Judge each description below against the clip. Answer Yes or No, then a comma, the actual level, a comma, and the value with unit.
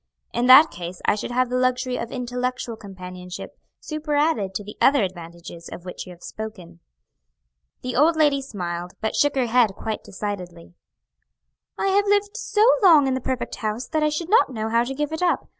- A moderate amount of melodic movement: No, wide, 7.2 semitones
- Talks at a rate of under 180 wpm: No, average, 190 wpm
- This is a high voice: Yes, high, 245 Hz